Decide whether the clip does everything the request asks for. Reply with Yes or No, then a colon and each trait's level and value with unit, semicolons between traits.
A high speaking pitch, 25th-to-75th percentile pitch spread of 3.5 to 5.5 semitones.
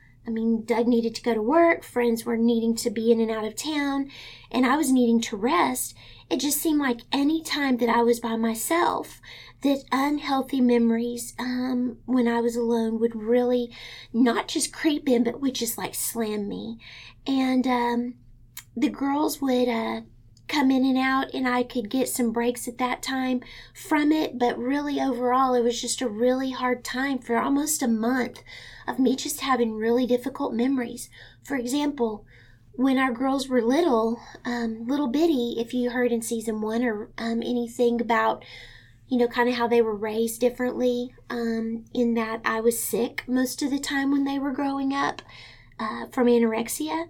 No: high, 245 Hz; narrow, 2.4 semitones